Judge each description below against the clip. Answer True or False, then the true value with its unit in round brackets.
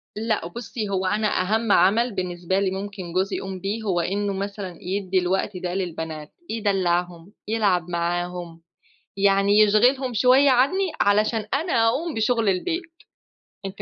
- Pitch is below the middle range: False (200 Hz)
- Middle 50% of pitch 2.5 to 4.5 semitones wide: True (3.5 semitones)